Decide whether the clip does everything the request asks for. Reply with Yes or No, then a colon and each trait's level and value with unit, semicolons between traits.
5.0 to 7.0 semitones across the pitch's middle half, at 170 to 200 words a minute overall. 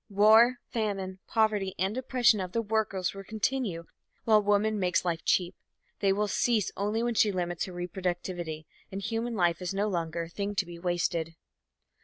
No: average, 3.5 semitones; average, 175 wpm